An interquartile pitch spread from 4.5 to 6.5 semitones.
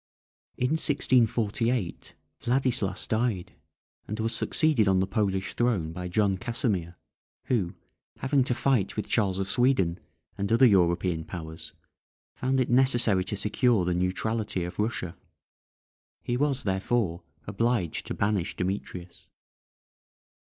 Yes: average, 4.8 semitones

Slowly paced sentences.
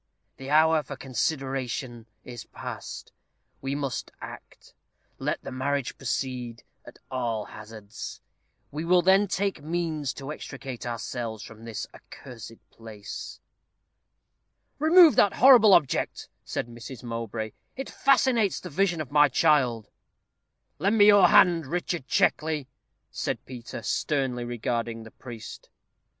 Yes: slow, 125 wpm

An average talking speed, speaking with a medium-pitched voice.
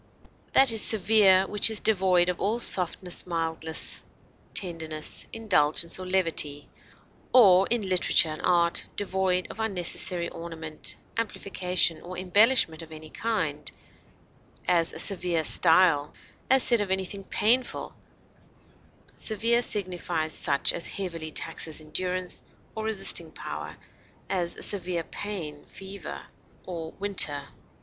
No: slow, 120 wpm; medium, 180 Hz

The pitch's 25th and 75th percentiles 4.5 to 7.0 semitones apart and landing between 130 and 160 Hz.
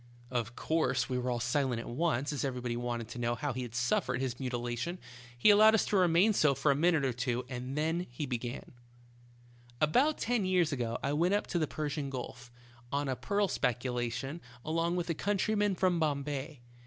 Yes: wide, 5.6 semitones; medium, 140 Hz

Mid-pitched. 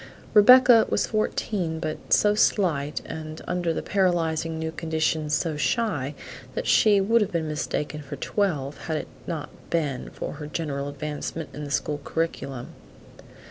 Yes: medium, 160 Hz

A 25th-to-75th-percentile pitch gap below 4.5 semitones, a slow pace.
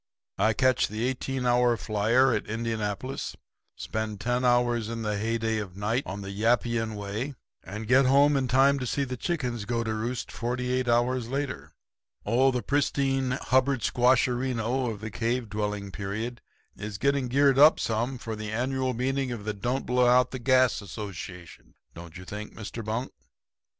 No: average, 3.0 semitones; average, 170 wpm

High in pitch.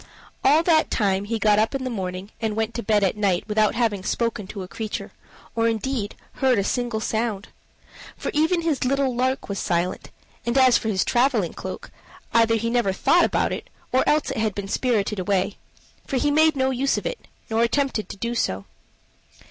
Yes: high, 230 Hz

